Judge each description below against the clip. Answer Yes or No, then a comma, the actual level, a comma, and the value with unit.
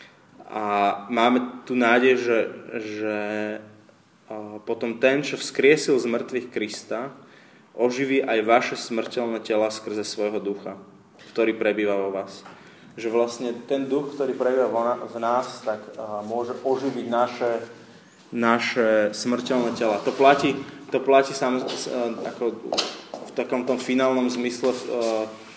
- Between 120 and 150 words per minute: Yes, average, 130 wpm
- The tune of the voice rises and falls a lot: No, average, 2.7 semitones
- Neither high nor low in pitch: No, low, 120 Hz